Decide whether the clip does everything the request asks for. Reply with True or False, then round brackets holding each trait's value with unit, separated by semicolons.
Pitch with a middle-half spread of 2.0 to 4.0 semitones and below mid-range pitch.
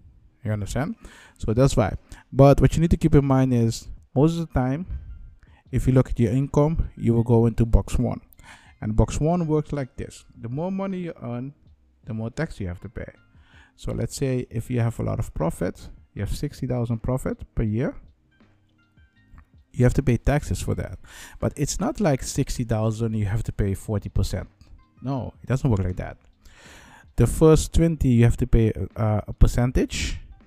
False (4.6 semitones; 115 Hz)